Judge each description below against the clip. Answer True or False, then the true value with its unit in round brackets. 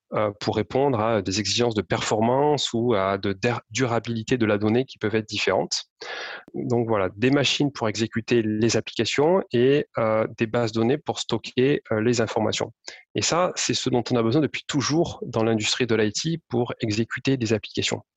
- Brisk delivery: False (170 wpm)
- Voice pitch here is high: False (115 Hz)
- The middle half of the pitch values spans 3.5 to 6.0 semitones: False (2.4 semitones)